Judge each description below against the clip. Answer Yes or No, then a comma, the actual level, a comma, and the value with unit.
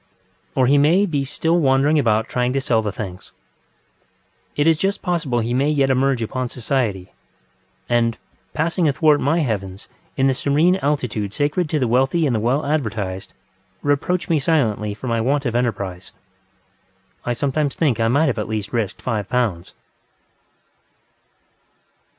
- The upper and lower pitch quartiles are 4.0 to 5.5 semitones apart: Yes, average, 4.7 semitones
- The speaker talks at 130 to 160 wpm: Yes, average, 155 wpm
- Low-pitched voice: Yes, low, 130 Hz